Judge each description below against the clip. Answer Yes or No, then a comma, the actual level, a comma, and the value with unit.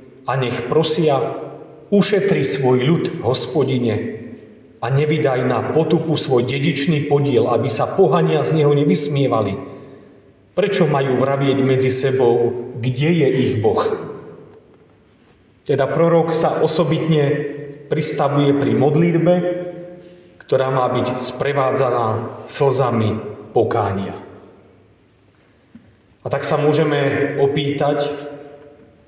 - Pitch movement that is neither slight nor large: Yes, average, 3.3 semitones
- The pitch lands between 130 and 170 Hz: Yes, medium, 140 Hz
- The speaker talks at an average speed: No, slow, 95 wpm